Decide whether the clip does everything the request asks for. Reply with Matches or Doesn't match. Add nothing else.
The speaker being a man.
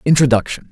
Matches